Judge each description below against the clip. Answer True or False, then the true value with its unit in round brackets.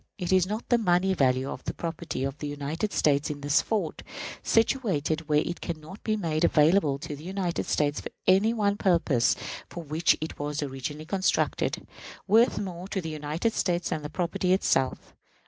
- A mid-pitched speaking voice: True (165 Hz)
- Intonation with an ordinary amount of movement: True (4.4 semitones)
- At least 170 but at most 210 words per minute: True (180 wpm)